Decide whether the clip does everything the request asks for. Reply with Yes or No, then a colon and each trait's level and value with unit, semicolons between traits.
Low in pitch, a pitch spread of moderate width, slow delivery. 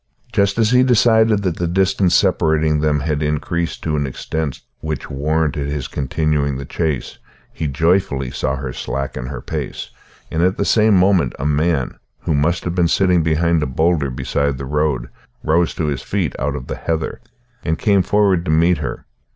No: very low, 80 Hz; average, 3.8 semitones; average, 185 wpm